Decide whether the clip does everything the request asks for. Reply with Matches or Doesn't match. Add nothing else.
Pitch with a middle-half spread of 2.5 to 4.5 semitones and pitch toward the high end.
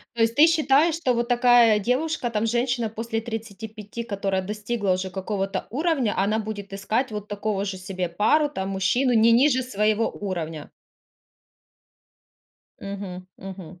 Matches